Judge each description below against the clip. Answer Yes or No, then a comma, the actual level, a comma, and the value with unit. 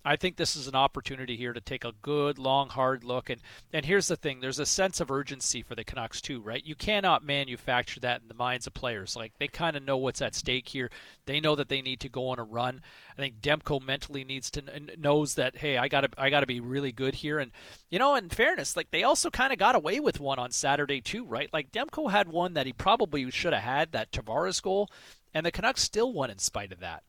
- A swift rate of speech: Yes, fast, 255 wpm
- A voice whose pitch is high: No, low, 135 Hz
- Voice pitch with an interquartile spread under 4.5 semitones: Yes, average, 2.8 semitones